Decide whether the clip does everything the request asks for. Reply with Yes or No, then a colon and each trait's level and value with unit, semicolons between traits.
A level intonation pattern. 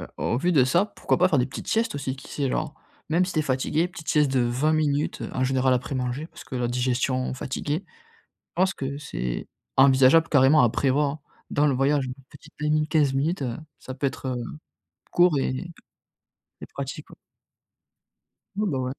No: average, 3.0 semitones